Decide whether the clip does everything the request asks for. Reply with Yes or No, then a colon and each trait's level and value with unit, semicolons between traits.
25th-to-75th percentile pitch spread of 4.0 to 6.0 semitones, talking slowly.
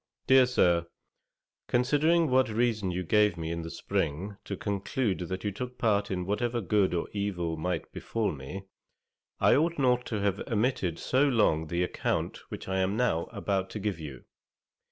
No: wide, 5.5 semitones; average, 175 wpm